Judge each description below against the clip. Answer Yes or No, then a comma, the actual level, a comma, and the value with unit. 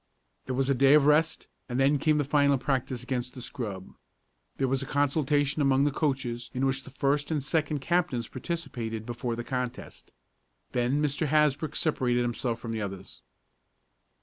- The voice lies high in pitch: No, low, 135 Hz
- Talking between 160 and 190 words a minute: Yes, average, 175 wpm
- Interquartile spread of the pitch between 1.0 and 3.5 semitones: Yes, average, 3.0 semitones